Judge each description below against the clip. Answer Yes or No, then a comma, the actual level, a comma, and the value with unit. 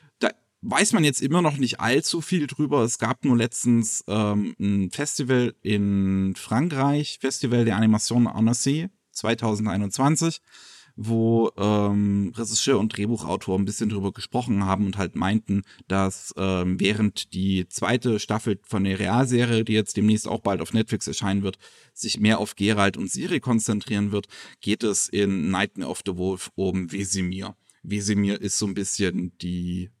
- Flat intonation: No, average, 3.2 semitones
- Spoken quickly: No, average, 155 wpm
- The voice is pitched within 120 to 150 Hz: No, low, 105 Hz